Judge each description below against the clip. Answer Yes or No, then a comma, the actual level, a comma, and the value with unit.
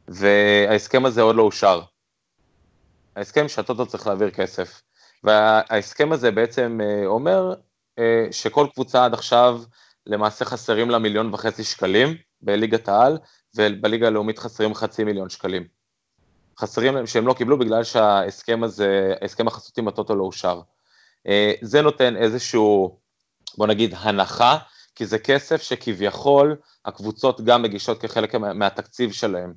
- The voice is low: Yes, low, 110 Hz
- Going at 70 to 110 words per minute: No, average, 125 wpm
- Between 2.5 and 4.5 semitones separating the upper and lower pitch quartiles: Yes, average, 2.9 semitones